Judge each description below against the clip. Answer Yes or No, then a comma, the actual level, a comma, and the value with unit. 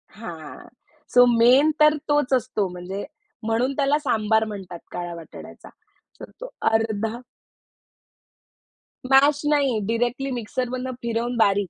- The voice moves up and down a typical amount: Yes, average, 4.2 semitones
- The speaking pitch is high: Yes, high, 230 Hz